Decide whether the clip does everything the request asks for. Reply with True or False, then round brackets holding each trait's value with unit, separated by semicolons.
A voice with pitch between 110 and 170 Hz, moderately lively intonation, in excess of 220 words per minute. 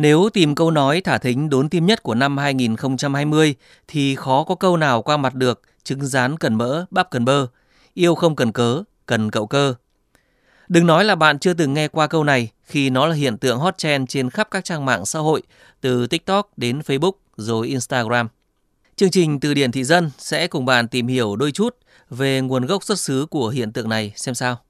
False (140 Hz; 4.6 semitones; 215 wpm)